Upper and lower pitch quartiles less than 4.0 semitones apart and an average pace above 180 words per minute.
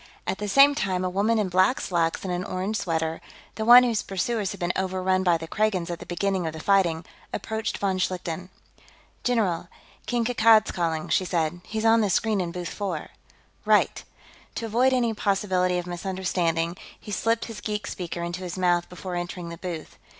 Yes: average, 3.5 semitones; average, 190 wpm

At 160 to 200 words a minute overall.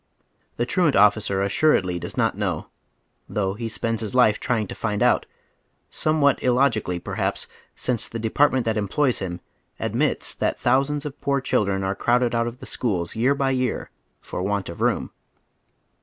Yes: average, 165 wpm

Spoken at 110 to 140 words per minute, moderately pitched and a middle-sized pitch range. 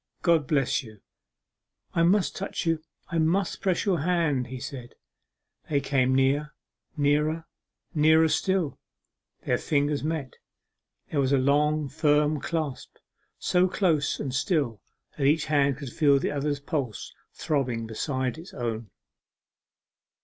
Yes: slow, 135 wpm; medium, 145 Hz; average, 3.1 semitones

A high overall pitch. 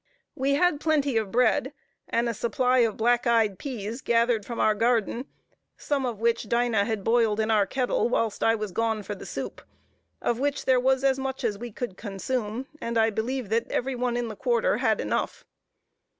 Yes: high, 235 Hz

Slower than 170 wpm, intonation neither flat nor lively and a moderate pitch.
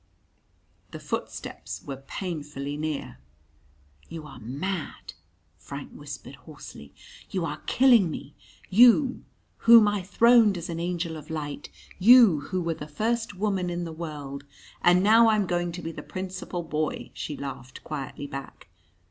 Yes: average, 150 wpm; average, 5.0 semitones; medium, 165 Hz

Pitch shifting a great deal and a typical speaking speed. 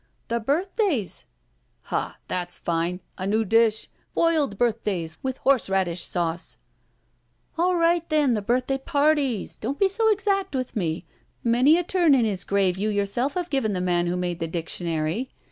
Yes: wide, 8.4 semitones; average, 165 wpm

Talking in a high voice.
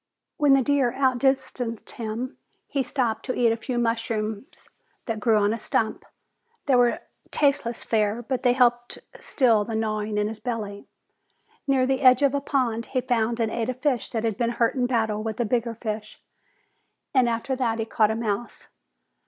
Yes: high, 235 Hz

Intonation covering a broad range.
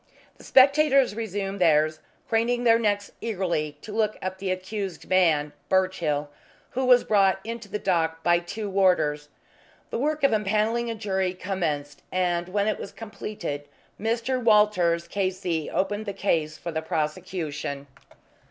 No: average, 4.3 semitones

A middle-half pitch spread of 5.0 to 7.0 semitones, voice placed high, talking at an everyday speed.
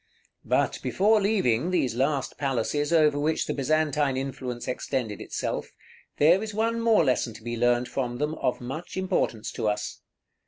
No: wide, 5.4 semitones; medium, 140 Hz; average, 170 wpm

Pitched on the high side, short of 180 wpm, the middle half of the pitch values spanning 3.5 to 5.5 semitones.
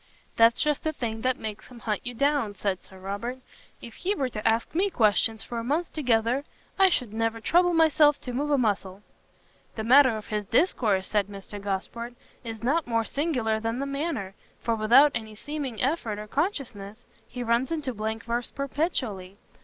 No: high, 235 Hz; average, 185 wpm; average, 4.7 semitones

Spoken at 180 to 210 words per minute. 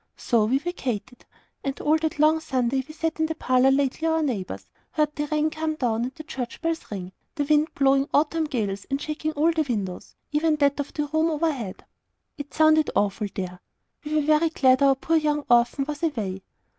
Yes: average, 200 wpm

